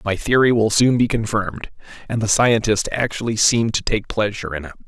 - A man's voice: Yes, male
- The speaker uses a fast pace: No, average, 195 wpm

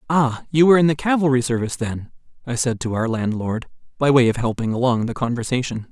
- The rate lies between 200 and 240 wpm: Yes, fast, 205 wpm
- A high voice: No, low, 125 Hz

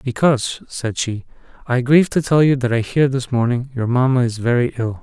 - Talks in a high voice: No, low, 125 Hz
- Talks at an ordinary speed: No, fast, 215 wpm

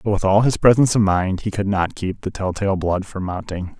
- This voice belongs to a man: Yes, male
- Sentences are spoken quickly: Yes, fast, 270 wpm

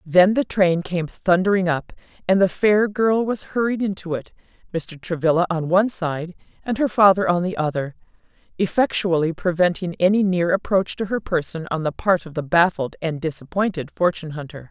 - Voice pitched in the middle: Yes, medium, 180 Hz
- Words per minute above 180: No, average, 175 wpm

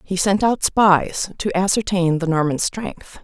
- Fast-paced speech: No, average, 165 wpm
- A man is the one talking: No, female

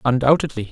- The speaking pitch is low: Yes, low, 130 Hz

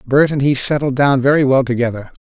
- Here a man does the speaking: Yes, male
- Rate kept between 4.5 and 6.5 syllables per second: Yes, 6.0 syllables/s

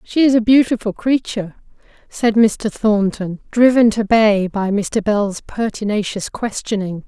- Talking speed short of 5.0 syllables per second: Yes, 4.2 syllables/s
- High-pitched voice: Yes, high, 215 Hz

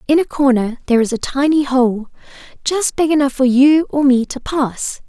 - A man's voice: No, female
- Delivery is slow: No, average, 200 wpm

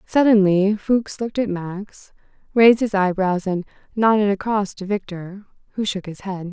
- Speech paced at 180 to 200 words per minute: No, average, 155 wpm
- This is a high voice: Yes, high, 200 Hz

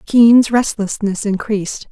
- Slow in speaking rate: Yes, slow, 95 wpm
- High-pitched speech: Yes, high, 215 Hz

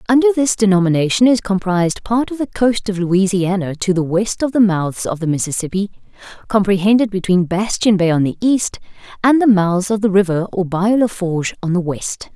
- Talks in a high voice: Yes, high, 200 Hz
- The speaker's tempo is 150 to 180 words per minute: No, average, 195 wpm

